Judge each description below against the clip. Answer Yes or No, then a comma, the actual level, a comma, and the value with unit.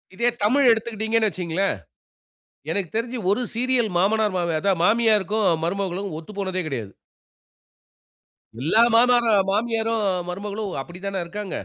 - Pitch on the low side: No, high, 205 Hz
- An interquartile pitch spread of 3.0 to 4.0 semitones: Yes, average, 3.4 semitones